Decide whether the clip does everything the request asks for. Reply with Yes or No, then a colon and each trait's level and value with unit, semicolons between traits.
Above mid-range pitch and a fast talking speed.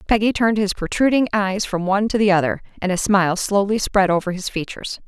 Yes: high, 200 Hz; fast, 215 wpm